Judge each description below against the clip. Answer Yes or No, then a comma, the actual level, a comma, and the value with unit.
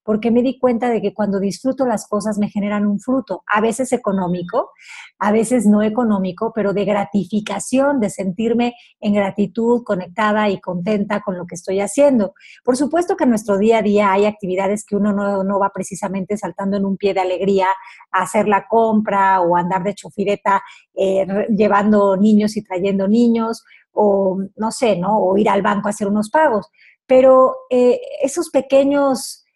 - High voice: Yes, high, 205 Hz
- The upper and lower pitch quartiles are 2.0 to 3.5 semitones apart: Yes, average, 2.7 semitones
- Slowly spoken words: No, average, 175 wpm